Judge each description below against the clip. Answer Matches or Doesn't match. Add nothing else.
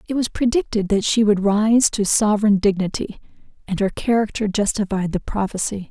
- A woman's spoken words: Matches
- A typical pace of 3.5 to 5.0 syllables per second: Doesn't match